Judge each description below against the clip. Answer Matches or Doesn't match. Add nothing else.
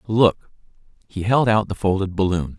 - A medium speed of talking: Matches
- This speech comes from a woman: Doesn't match